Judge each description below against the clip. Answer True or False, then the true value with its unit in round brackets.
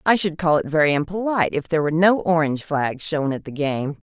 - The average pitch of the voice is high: False (160 Hz)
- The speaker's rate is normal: False (235 wpm)